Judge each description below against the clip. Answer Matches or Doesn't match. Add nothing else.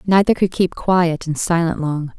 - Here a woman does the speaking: Matches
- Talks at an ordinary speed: Matches